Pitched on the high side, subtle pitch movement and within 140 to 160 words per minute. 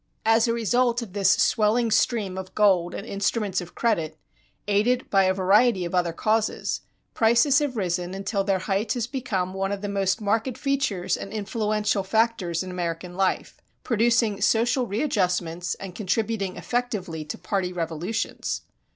No: high, 200 Hz; average, 3.8 semitones; average, 155 wpm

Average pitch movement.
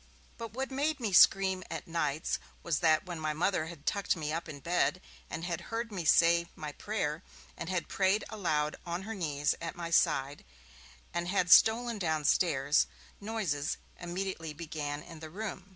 Yes: average, 3.9 semitones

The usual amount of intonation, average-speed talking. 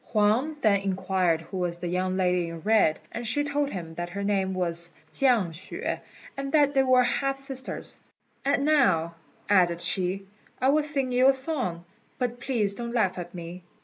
No: wide, 6.9 semitones; average, 180 wpm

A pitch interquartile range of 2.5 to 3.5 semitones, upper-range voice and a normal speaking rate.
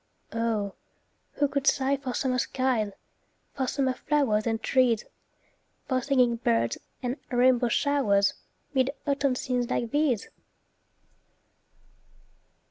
No: average, 3.0 semitones; very high, 255 Hz; slow, 110 wpm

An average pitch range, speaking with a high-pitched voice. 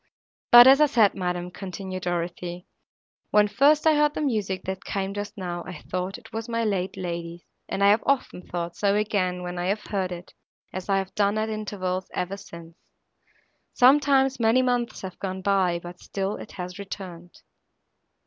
Yes: average, 3.4 semitones; high, 195 Hz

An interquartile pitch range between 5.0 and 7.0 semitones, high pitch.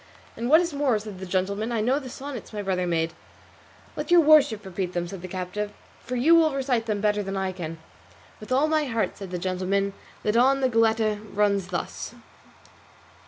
Yes: wide, 5.4 semitones; high, 215 Hz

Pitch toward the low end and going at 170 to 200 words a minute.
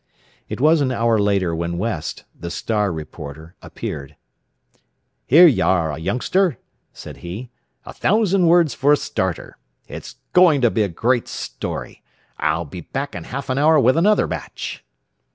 No: low, 115 Hz; average, 155 wpm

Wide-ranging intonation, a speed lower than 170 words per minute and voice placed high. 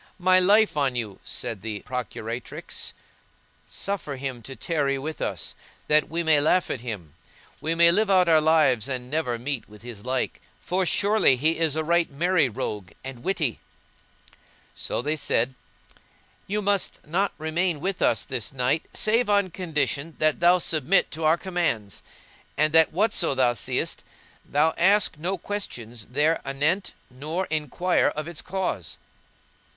No: wide, 5.7 semitones; average, 155 wpm; medium, 155 Hz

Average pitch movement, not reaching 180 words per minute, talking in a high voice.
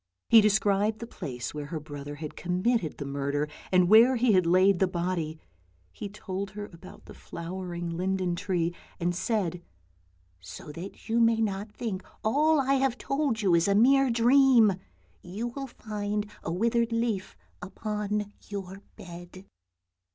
Yes: average, 4.7 semitones; average, 160 wpm; high, 195 Hz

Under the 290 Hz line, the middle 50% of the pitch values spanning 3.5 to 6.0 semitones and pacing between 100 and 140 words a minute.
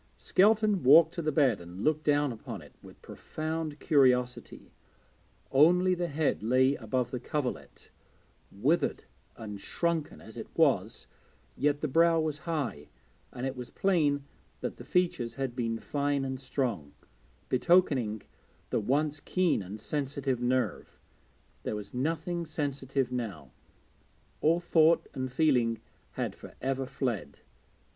Yes: medium, 140 Hz; average, 4.2 semitones; slow, 135 wpm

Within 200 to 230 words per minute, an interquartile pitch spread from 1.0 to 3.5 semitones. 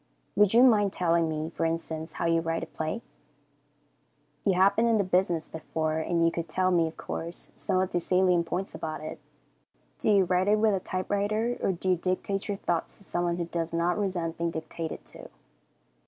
Yes: fast, 205 wpm; average, 2.8 semitones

